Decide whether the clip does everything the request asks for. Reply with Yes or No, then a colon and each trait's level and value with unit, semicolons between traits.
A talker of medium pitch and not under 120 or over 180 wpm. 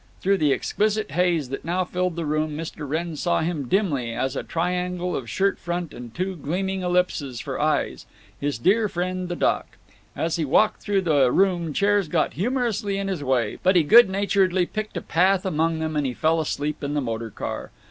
No: medium, 175 Hz; average, 200 wpm